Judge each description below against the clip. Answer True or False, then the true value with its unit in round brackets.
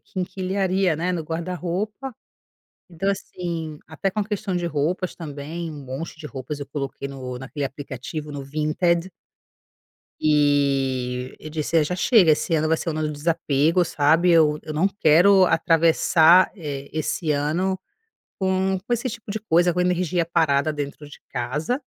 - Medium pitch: True (160 Hz)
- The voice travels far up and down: False (3.8 semitones)